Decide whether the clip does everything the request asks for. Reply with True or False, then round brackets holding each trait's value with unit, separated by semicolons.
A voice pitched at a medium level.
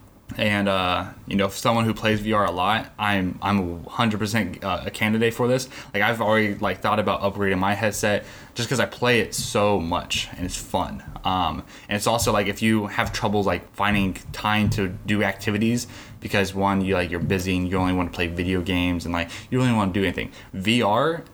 False (105 Hz)